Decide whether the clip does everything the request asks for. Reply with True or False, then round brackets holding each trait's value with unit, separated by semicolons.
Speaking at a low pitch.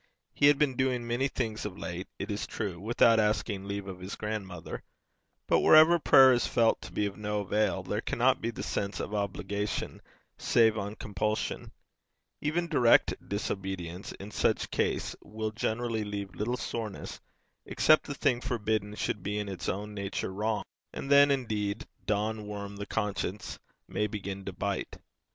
True (105 Hz)